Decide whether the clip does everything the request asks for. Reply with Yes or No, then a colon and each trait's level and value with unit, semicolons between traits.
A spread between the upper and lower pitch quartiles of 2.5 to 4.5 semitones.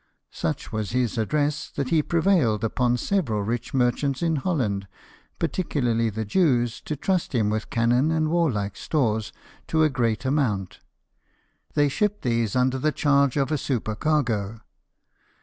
No: average, 5.2 semitones